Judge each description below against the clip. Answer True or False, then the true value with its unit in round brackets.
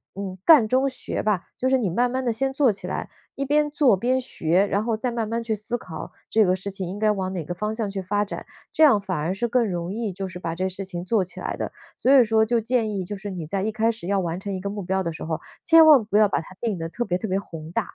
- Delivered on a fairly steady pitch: False (4.1 semitones)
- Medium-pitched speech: False (205 Hz)